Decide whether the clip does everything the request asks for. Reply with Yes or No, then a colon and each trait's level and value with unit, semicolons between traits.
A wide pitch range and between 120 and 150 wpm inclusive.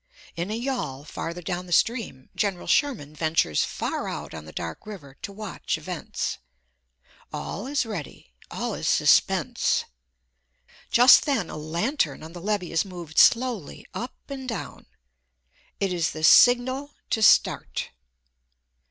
Yes: wide, 7.2 semitones; average, 140 wpm